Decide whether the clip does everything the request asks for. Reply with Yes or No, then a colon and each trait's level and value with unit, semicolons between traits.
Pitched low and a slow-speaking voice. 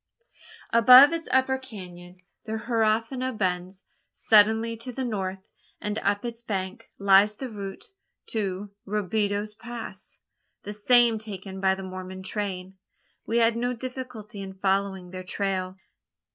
No: high, 210 Hz; slow, 130 wpm